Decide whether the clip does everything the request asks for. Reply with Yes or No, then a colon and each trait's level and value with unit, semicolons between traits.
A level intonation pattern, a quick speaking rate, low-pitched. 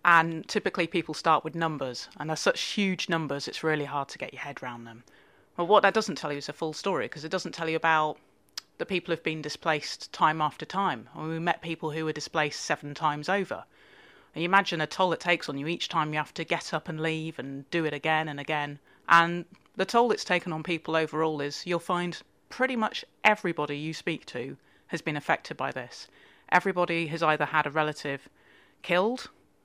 No: narrow, 2.3 semitones; fast, 220 wpm; medium, 160 Hz